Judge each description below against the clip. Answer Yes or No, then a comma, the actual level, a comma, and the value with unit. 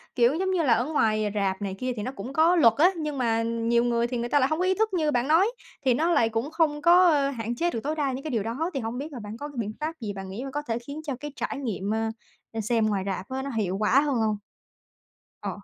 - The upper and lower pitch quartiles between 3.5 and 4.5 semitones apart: No, average, 5.0 semitones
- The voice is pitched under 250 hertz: No, very high, 255 Hz